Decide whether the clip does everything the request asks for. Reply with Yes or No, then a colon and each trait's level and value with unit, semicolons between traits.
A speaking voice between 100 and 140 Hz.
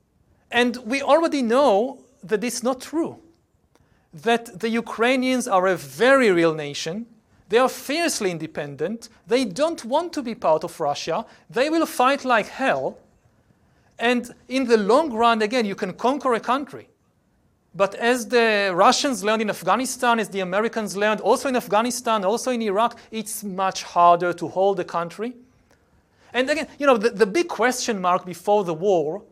No: high, 230 Hz